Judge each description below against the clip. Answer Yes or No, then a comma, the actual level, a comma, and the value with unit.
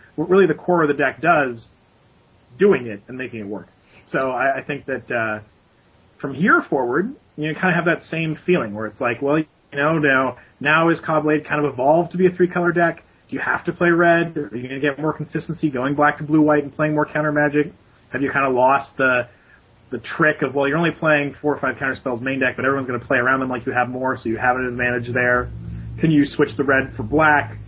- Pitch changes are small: No, average, 3.6 semitones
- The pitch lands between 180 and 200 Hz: No, medium, 140 Hz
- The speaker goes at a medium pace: No, fast, 255 wpm